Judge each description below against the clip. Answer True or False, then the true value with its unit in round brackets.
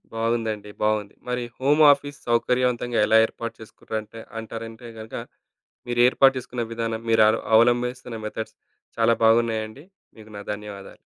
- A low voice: True (115 Hz)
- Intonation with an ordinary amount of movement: False (1.8 semitones)